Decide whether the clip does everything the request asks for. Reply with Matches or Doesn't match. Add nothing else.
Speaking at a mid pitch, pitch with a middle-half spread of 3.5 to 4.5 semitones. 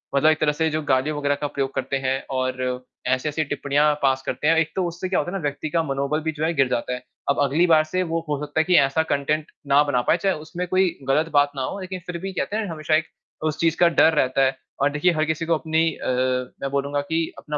Doesn't match